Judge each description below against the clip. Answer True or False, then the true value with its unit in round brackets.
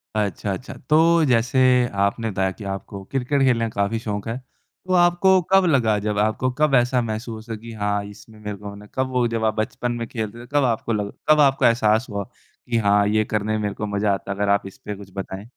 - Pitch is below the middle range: True (110 Hz)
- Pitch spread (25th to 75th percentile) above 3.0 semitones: True (3.5 semitones)